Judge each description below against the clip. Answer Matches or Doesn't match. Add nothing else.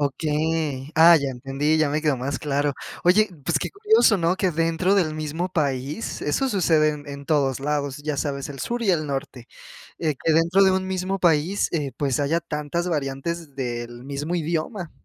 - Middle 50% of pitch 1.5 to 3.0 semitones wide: Doesn't match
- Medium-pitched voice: Matches